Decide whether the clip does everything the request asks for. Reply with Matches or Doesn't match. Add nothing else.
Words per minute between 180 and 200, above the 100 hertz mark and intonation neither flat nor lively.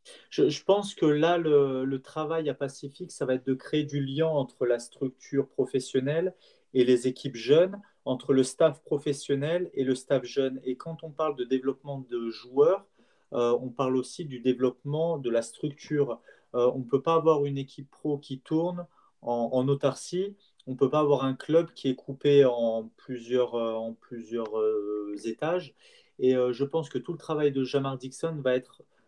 Matches